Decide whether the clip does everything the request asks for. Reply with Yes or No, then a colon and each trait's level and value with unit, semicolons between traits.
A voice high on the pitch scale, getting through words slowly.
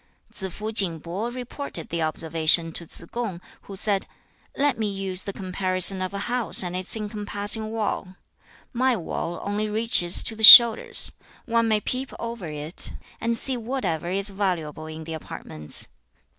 No: high, 200 Hz; average, 165 wpm